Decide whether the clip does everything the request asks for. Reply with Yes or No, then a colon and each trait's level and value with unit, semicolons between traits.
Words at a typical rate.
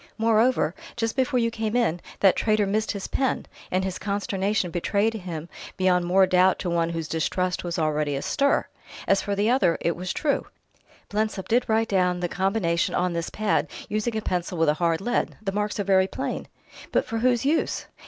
Yes: average, 190 wpm